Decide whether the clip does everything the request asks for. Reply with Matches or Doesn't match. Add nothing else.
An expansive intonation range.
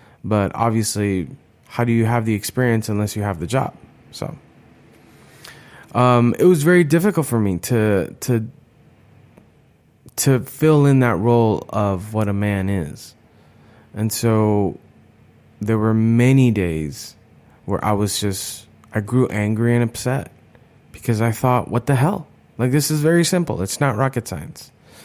Doesn't match